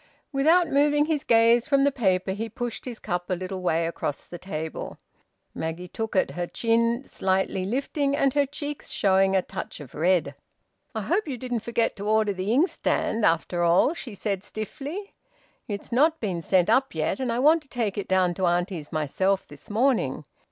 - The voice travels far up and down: Yes, wide, 6.5 semitones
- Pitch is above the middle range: Yes, high, 215 Hz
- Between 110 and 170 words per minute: No, average, 185 wpm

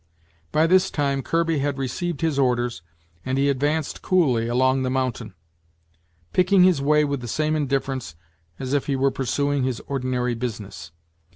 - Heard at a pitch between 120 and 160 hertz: Yes, low, 135 Hz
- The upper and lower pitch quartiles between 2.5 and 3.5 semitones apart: Yes, average, 3.2 semitones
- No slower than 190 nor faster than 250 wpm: No, average, 160 wpm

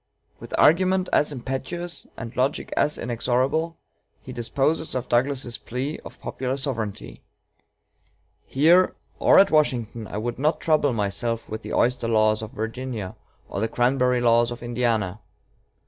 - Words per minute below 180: Yes, average, 140 wpm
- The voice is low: Yes, low, 125 Hz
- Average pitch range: Yes, average, 3.7 semitones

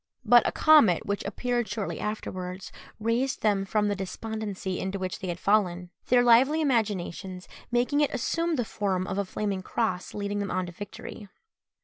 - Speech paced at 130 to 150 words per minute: No, average, 170 wpm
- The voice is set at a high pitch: Yes, high, 205 Hz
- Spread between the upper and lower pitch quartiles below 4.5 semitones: Yes, average, 4.0 semitones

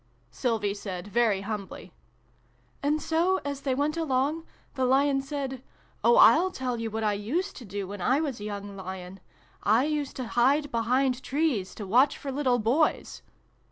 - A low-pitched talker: No, very high, 255 Hz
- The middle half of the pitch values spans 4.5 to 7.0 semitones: Yes, wide, 5.5 semitones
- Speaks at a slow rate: No, average, 185 wpm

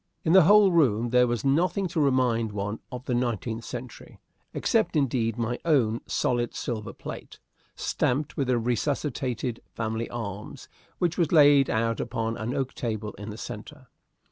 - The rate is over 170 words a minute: No, average, 160 wpm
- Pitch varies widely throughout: No, average, 3.7 semitones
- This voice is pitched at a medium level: No, low, 120 Hz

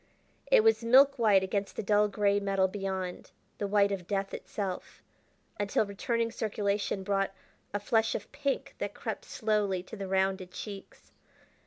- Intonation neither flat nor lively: No, narrow, 2.0 semitones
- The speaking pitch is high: Yes, high, 200 Hz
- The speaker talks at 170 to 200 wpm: No, average, 155 wpm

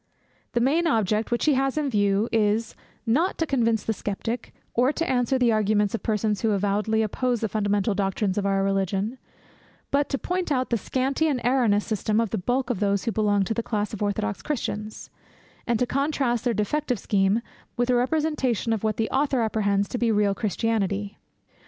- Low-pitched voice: No, high, 225 Hz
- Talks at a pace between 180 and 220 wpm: Yes, average, 195 wpm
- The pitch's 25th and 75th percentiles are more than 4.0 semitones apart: No, average, 3.6 semitones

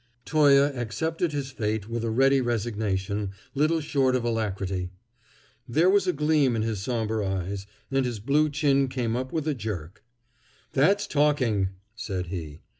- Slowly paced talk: No, average, 155 wpm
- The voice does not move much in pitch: No, wide, 5.6 semitones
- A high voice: No, low, 120 Hz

